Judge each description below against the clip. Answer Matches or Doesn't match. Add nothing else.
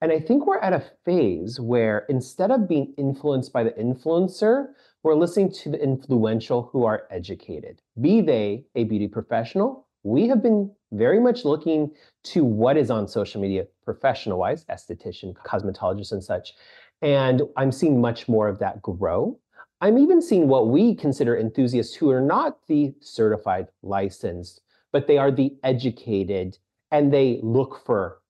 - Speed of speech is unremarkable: Matches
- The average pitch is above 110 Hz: Matches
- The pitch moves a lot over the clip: Matches